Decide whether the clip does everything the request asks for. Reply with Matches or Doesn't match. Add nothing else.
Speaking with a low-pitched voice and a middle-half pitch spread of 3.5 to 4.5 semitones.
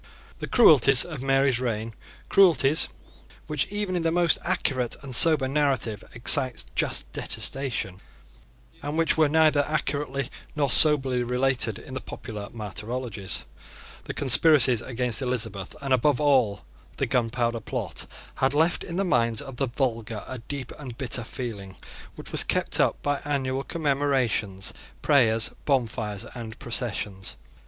Matches